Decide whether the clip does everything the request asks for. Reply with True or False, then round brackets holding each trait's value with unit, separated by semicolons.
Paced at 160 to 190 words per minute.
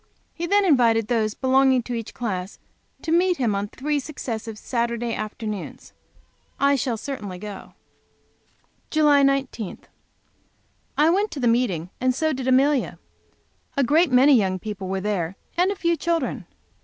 False (150 wpm)